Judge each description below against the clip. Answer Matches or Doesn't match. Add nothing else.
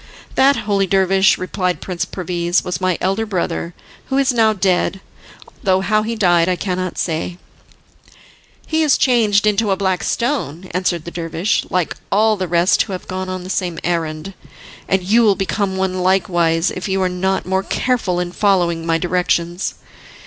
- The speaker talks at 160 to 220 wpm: Matches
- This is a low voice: Doesn't match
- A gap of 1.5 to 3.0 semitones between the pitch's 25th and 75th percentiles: Matches